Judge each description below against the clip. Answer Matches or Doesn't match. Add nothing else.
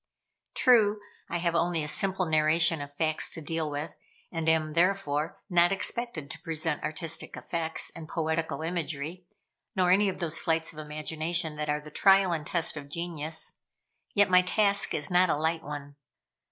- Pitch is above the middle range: Doesn't match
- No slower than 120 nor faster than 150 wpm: Doesn't match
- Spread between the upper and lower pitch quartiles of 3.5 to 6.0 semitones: Doesn't match